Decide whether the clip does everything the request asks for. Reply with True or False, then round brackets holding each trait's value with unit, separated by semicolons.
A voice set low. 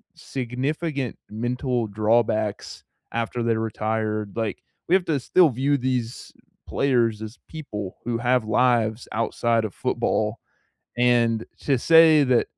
True (120 Hz)